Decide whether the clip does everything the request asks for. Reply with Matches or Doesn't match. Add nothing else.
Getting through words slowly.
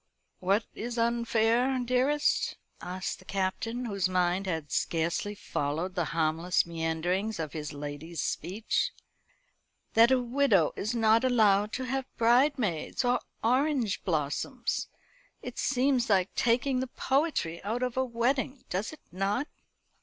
Matches